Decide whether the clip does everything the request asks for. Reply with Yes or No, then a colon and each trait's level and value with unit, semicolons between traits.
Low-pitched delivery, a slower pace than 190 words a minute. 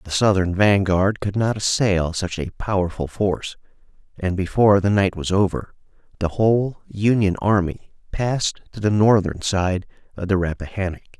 Yes: very low, 95 Hz; average, 150 wpm